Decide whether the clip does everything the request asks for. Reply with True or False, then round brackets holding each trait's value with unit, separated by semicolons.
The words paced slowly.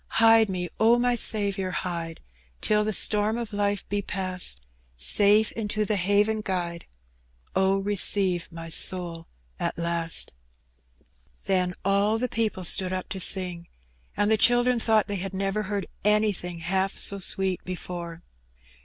False (145 wpm)